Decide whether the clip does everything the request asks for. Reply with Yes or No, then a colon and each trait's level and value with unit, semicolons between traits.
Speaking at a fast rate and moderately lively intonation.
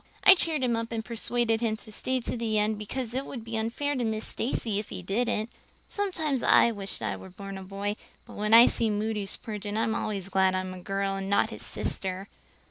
Yes: fast, 225 wpm; average, 3.0 semitones